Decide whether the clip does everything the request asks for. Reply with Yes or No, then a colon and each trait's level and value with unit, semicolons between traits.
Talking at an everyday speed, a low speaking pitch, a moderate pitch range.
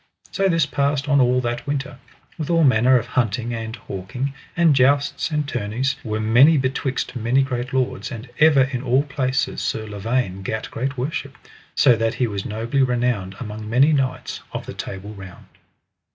Yes: average, 175 wpm; low, 125 Hz; average, 3.7 semitones